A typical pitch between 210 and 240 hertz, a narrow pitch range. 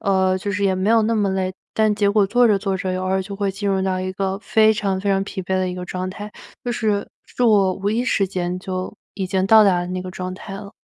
No: high, 195 Hz; narrow, 1.8 semitones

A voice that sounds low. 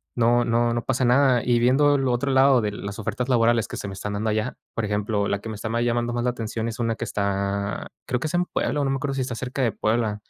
Yes: low, 120 Hz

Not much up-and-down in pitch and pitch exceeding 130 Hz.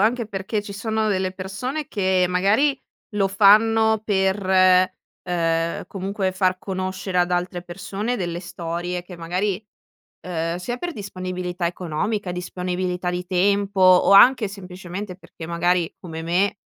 Yes: narrow, 2.2 semitones; medium, 185 Hz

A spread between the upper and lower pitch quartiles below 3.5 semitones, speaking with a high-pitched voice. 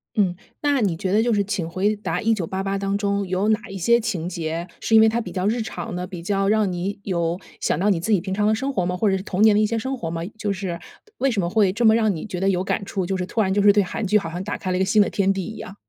Yes: average, 2.9 semitones; high, 195 Hz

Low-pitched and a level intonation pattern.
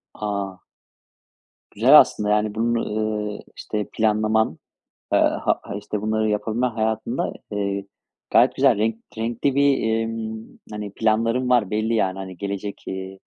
Yes: low, 110 Hz; narrow, 1.7 semitones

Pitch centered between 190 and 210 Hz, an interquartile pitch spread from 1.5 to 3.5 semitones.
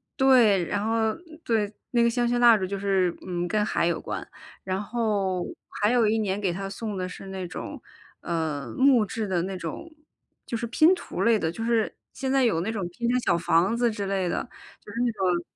No: high, 205 Hz; average, 4.2 semitones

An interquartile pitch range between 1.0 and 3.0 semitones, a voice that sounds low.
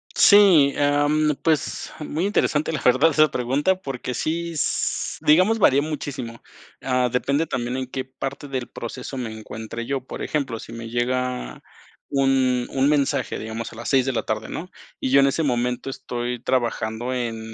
No: average, 3.4 semitones; low, 130 Hz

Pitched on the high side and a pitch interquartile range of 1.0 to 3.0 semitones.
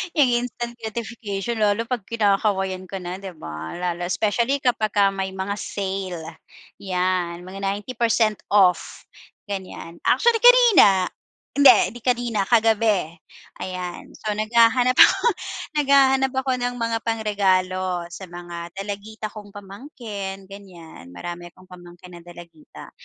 No: high, 200 Hz; average, 4.0 semitones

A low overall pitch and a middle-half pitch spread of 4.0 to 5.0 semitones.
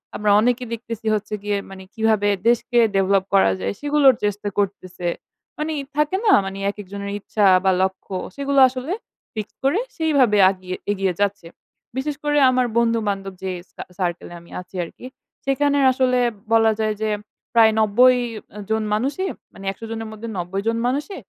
No: high, 220 Hz; average, 4.5 semitones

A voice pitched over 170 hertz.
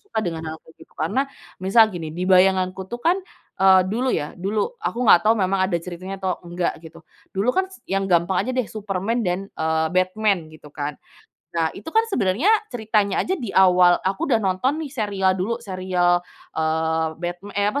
Yes: high, 190 Hz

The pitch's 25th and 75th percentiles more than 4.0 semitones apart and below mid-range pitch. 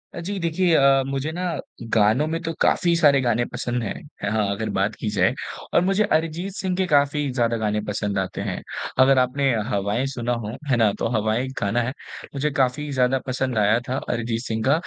Yes: average, 5.1 semitones; low, 130 Hz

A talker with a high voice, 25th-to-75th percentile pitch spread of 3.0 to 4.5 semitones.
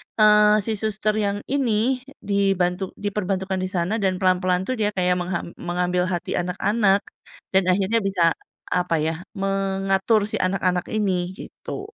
No: high, 195 Hz; narrow, 2.5 semitones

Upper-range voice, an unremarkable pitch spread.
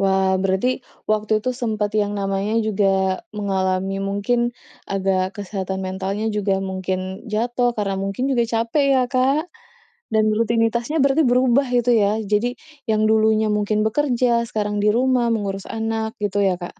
Yes: high, 215 Hz; average, 3.4 semitones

